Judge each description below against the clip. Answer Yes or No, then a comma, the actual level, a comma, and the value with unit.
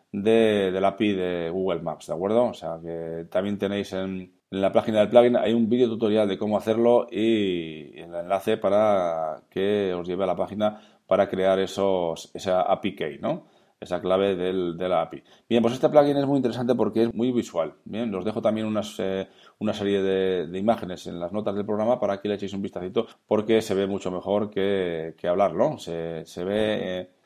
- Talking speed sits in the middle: No, fast, 210 wpm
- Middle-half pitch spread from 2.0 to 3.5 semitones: Yes, average, 2.8 semitones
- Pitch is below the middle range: Yes, low, 100 Hz